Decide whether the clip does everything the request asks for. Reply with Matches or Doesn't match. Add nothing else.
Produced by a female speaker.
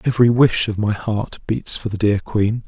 Doesn't match